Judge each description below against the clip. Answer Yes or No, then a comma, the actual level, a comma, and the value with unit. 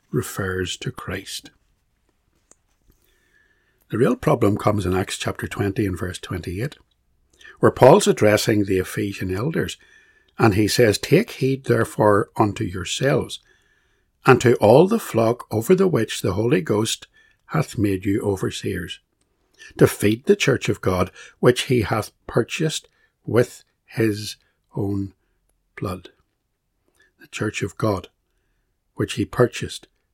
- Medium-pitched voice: No, low, 105 Hz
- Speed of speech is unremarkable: No, slow, 130 wpm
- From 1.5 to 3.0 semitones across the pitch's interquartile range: No, average, 4.0 semitones